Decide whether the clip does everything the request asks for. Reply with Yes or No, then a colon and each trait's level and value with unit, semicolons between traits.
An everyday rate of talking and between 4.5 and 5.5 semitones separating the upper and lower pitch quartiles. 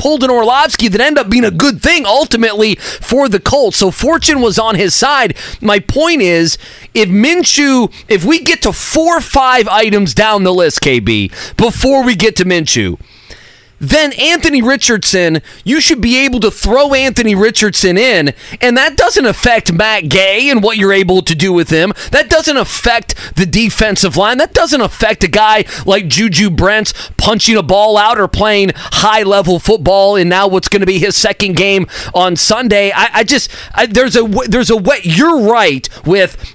Yes: average, 185 wpm; average, 4.9 semitones